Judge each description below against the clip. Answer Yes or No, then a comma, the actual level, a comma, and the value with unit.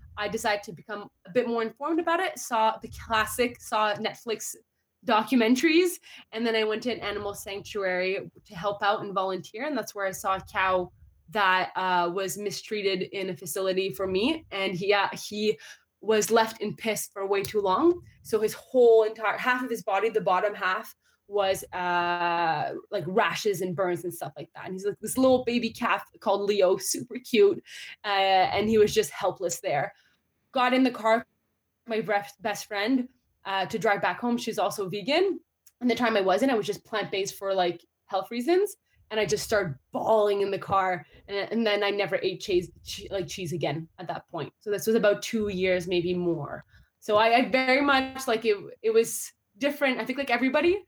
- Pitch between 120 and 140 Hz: No, high, 205 Hz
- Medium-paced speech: Yes, average, 195 wpm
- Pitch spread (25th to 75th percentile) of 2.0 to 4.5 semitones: Yes, average, 3.4 semitones